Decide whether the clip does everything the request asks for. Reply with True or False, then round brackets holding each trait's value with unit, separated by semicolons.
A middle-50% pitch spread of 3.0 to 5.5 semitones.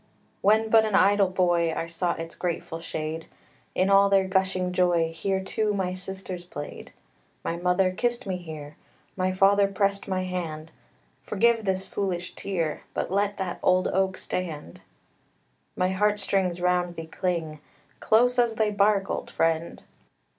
False (2.4 semitones)